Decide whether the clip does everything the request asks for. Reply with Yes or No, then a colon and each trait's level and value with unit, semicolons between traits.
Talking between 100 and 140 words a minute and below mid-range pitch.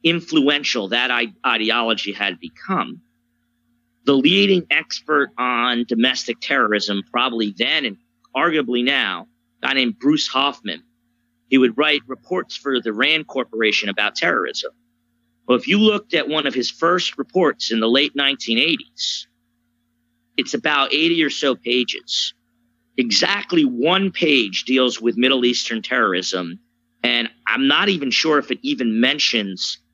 Yes: slow, 135 wpm; low, 120 Hz